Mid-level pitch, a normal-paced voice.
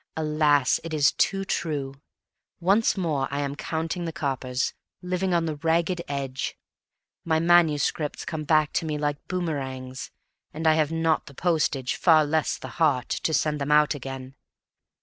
Yes: medium, 155 Hz; average, 160 wpm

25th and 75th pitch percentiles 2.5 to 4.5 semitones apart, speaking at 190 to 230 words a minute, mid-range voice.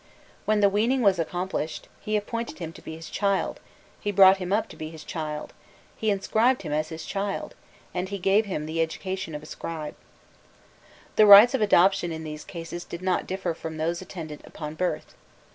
Yes: average, 3.9 semitones; average, 195 wpm; medium, 180 Hz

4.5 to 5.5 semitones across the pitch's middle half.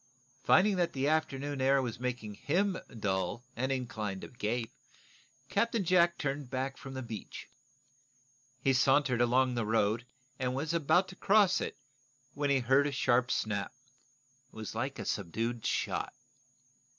No: average, 3.8 semitones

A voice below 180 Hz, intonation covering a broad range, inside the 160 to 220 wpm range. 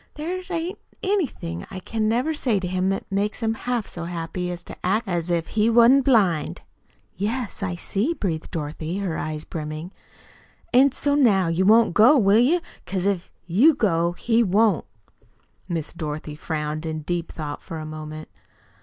No: high, 190 Hz; wide, 5.9 semitones; average, 170 wpm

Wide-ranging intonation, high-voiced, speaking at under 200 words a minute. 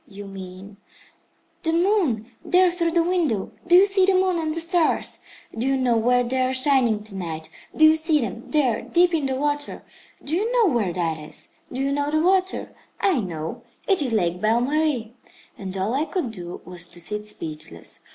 No: wide, 8.4 semitones; very high, 260 Hz; fast, 205 wpm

